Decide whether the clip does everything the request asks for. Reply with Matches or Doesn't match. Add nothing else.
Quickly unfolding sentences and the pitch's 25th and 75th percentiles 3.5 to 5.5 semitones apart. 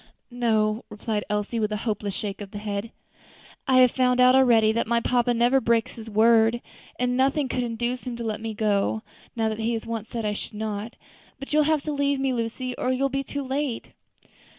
Doesn't match